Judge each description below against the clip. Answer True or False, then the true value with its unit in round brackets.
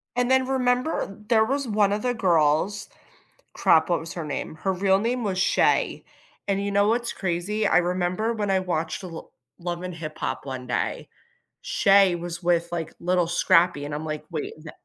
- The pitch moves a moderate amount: True (3.8 semitones)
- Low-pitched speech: False (185 Hz)